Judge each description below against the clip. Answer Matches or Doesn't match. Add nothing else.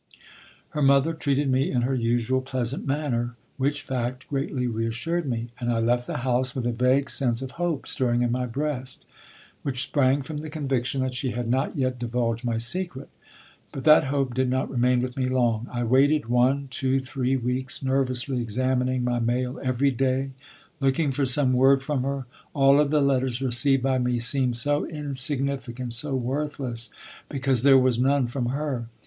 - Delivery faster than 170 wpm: Matches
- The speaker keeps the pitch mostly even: Matches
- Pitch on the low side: Matches